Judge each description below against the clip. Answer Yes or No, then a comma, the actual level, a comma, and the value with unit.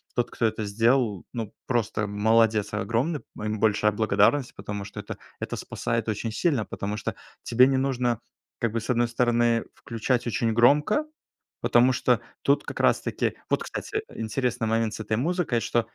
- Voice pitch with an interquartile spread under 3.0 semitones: Yes, narrow, 2.5 semitones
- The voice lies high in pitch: No, low, 115 Hz